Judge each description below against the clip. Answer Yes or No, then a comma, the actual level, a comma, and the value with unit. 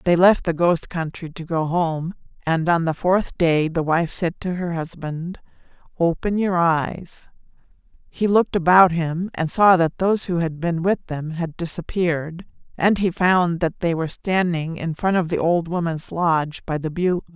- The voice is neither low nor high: Yes, medium, 170 Hz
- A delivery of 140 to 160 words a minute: No, average, 185 wpm